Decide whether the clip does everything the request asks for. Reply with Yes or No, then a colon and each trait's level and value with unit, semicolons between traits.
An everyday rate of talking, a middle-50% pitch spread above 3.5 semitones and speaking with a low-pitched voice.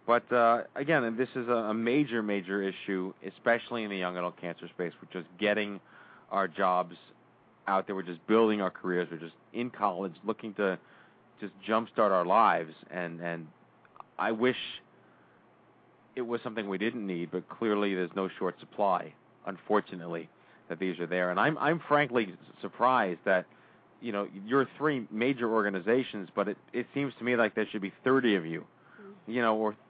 Yes: average, 175 wpm; average, 4.5 semitones; low, 105 Hz